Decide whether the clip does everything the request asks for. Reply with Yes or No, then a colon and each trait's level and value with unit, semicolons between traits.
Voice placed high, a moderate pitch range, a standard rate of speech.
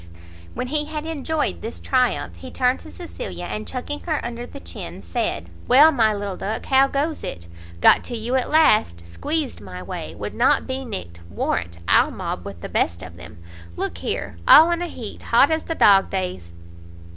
No: very high, 250 Hz; wide, 8.3 semitones; average, 190 wpm